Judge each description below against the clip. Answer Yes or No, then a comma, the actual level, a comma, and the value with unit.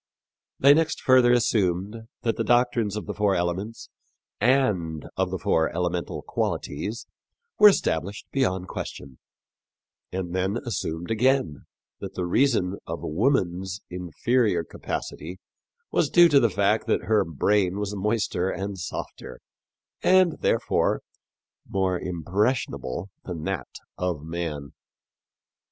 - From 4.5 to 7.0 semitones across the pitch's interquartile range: Yes, average, 4.9 semitones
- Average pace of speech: No, slow, 120 wpm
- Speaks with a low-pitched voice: Yes, very low, 95 Hz